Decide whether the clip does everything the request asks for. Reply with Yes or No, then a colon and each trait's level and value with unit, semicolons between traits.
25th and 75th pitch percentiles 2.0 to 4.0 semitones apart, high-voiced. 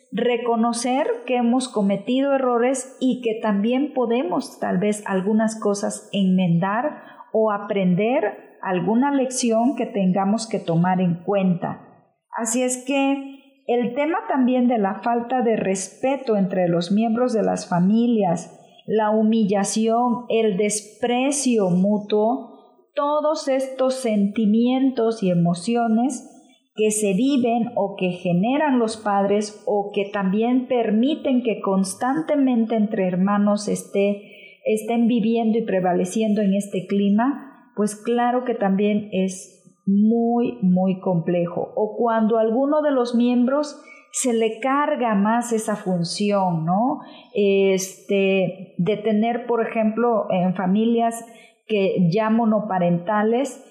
Yes: average, 3.6 semitones; high, 225 Hz